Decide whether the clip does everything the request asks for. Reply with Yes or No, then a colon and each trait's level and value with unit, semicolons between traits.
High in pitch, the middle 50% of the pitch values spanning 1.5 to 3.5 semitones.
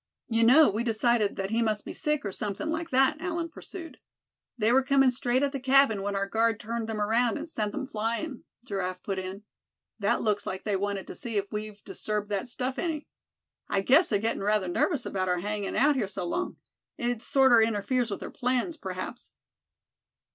No: high, 225 Hz; average, 4.6 semitones